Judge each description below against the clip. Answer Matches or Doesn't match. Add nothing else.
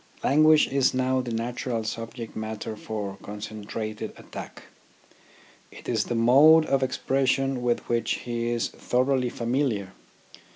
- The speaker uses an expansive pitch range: Doesn't match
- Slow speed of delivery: Matches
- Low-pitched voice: Matches